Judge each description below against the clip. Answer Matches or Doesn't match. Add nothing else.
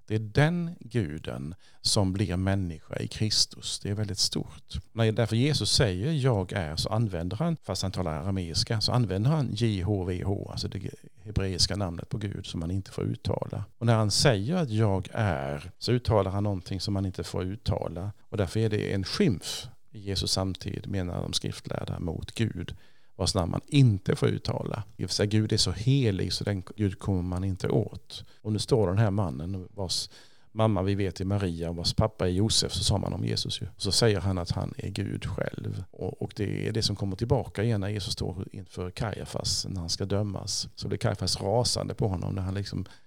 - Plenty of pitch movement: Doesn't match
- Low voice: Matches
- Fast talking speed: Matches